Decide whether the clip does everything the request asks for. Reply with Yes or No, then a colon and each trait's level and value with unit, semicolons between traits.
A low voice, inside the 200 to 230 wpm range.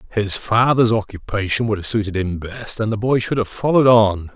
Yes: low, 110 Hz; fast, 205 wpm